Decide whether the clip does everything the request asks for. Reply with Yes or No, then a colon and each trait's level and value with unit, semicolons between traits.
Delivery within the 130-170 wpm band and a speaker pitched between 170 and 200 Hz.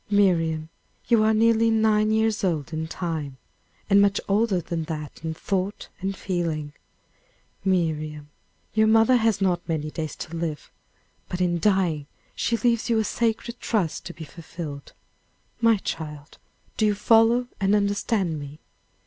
Yes: average, 150 wpm; high, 190 Hz